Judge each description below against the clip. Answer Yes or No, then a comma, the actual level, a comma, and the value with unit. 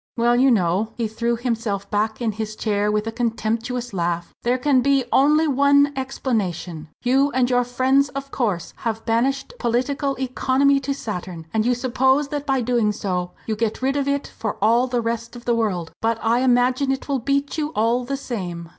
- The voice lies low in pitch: No, high, 240 Hz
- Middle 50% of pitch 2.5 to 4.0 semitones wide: Yes, average, 3.6 semitones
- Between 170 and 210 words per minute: Yes, average, 195 wpm